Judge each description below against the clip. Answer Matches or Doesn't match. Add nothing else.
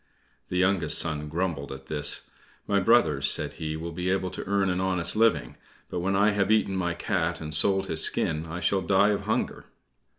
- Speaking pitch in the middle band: Doesn't match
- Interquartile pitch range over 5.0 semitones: Doesn't match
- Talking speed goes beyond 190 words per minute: Matches